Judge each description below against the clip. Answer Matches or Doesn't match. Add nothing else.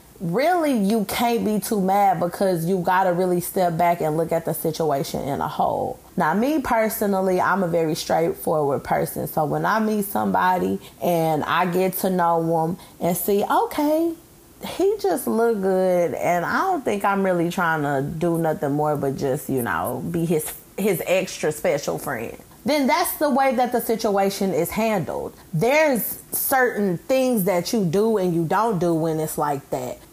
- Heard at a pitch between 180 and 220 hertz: Matches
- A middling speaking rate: Matches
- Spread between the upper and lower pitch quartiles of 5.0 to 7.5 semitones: Matches